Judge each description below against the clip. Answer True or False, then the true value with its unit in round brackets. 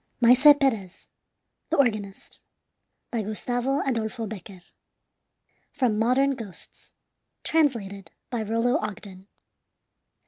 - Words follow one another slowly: True (90 wpm)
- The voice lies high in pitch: True (230 Hz)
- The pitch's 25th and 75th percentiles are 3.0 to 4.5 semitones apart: True (3.7 semitones)